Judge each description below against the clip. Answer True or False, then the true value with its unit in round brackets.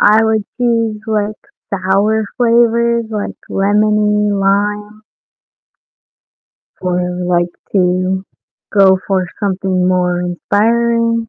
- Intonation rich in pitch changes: False (2.9 semitones)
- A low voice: False (205 Hz)